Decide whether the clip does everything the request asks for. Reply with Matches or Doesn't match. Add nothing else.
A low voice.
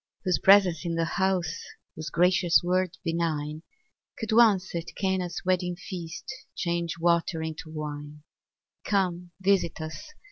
Doesn't match